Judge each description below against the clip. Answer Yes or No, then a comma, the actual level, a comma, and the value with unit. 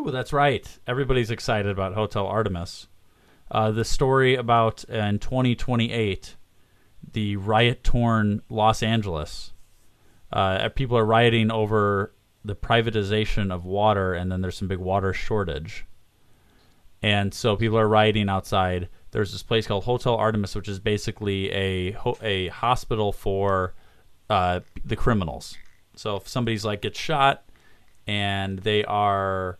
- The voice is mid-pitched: No, low, 105 Hz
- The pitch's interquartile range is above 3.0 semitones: No, average, 2.7 semitones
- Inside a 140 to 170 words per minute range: Yes, average, 145 wpm